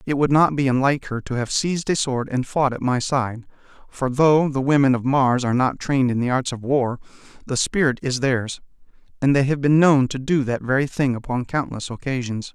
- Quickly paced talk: Yes, fast, 225 wpm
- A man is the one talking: Yes, male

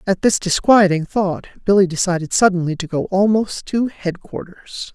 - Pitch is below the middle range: No, high, 190 Hz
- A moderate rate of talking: Yes, average, 145 wpm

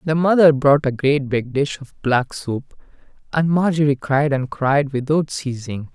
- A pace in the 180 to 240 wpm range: No, average, 170 wpm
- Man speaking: Yes, male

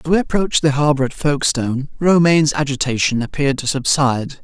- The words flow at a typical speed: Yes, average, 160 wpm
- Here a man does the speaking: Yes, male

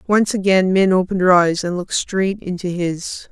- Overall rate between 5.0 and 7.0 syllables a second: Yes, 5.1 syllables/s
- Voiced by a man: No, female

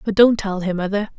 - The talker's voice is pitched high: Yes, high, 200 Hz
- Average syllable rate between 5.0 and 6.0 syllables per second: Yes, 5.9 syllables/s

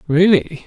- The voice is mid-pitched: Yes, medium, 165 Hz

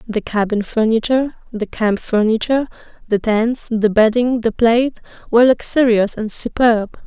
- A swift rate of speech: No, slow, 135 wpm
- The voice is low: No, high, 230 Hz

